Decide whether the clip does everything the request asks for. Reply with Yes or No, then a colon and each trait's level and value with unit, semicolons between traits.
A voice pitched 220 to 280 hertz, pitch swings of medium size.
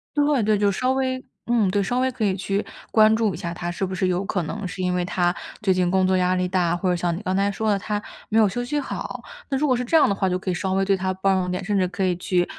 No: high, 195 Hz; average, 3.0 semitones